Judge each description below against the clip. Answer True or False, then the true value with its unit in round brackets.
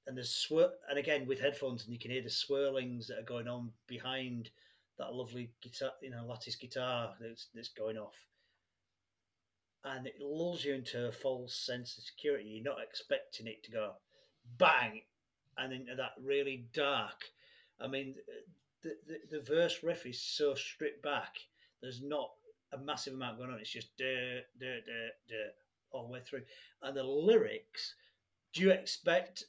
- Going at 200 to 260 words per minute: False (175 wpm)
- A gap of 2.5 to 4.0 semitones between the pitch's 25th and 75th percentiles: True (3.0 semitones)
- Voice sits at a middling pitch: False (130 Hz)